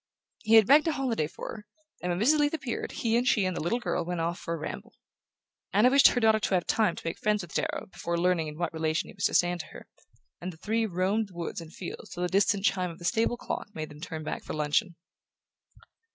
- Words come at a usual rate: No, fast, 255 wpm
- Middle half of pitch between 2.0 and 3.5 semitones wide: No, average, 4.8 semitones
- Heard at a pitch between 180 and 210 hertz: Yes, medium, 185 Hz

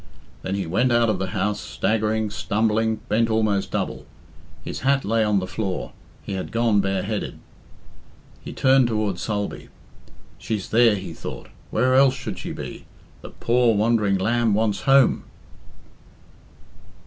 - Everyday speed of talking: Yes, average, 145 wpm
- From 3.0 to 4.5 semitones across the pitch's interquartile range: No, narrow, 2.6 semitones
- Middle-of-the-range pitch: No, low, 110 Hz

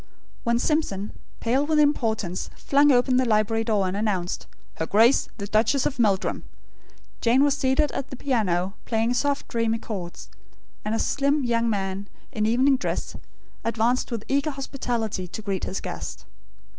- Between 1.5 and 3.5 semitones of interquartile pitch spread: No, average, 4.3 semitones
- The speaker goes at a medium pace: Yes, average, 160 wpm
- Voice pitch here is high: Yes, high, 230 Hz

